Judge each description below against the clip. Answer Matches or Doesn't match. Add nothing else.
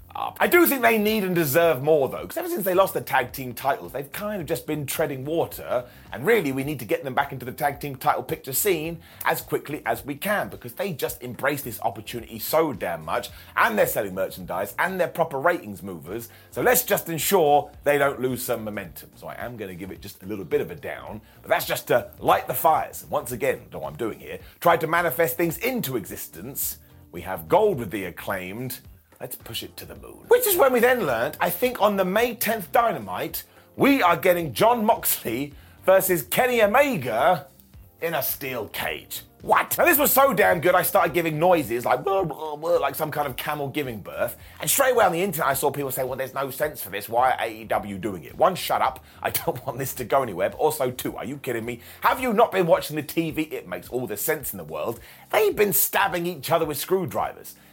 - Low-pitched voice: Doesn't match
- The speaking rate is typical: Doesn't match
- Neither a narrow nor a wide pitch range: Doesn't match